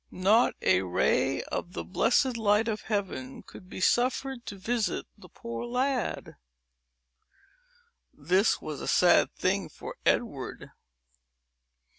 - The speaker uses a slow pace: Yes, slow, 120 wpm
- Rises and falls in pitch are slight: No, average, 4.8 semitones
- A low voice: No, high, 215 Hz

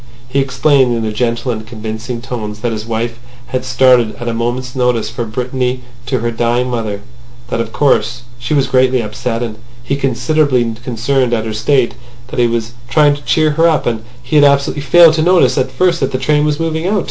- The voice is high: No, low, 125 Hz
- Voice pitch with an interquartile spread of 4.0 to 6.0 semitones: No, average, 3.1 semitones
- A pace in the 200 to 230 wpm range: Yes, fast, 205 wpm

